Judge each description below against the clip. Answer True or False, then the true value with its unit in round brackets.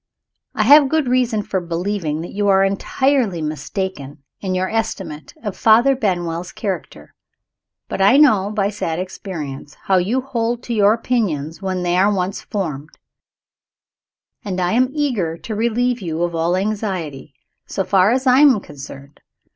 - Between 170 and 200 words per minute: False (155 wpm)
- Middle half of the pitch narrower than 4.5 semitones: False (5.1 semitones)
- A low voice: False (195 Hz)